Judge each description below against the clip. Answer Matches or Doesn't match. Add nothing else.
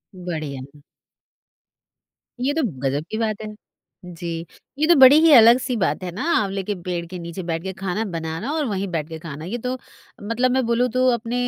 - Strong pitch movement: Matches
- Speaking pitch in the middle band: Doesn't match